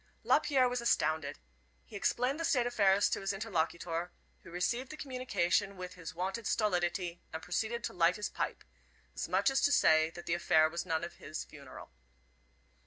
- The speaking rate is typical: Yes, average, 180 wpm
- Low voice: No, medium, 185 Hz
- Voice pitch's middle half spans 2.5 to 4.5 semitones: No, wide, 5.6 semitones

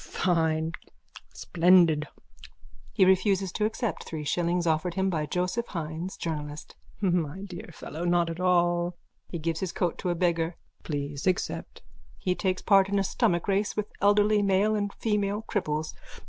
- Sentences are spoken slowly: No, average, 160 wpm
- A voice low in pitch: No, medium, 180 Hz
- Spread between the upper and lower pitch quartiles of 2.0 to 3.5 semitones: Yes, average, 3.1 semitones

